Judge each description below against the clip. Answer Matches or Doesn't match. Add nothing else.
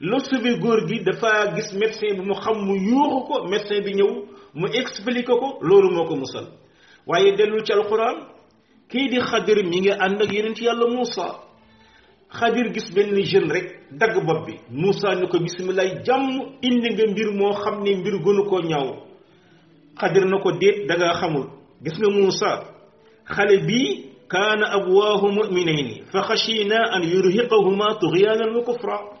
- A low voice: Doesn't match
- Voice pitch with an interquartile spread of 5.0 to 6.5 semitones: Doesn't match